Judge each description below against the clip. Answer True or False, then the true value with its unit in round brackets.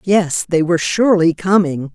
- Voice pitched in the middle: True (175 Hz)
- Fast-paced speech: False (155 wpm)